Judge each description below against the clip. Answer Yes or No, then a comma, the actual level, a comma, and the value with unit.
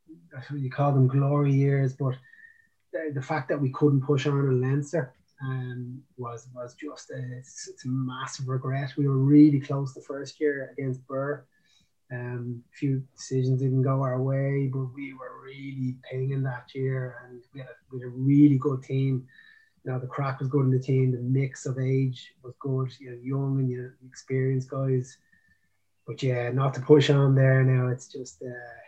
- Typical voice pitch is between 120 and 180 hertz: Yes, low, 135 Hz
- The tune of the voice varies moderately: No, narrow, 1.5 semitones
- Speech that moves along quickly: No, average, 190 wpm